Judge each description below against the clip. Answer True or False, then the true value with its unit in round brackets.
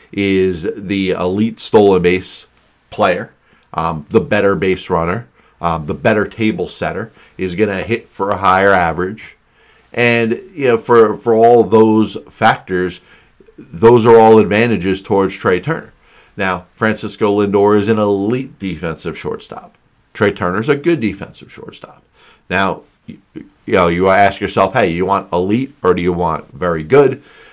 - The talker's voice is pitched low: True (100 Hz)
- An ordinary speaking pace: True (155 wpm)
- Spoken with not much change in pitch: False (3.4 semitones)